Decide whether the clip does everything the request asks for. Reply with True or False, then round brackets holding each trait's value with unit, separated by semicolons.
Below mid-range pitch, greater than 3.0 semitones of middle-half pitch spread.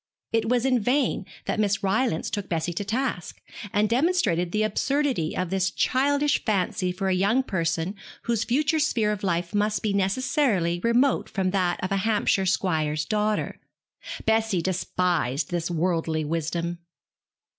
False (195 Hz; 4.9 semitones)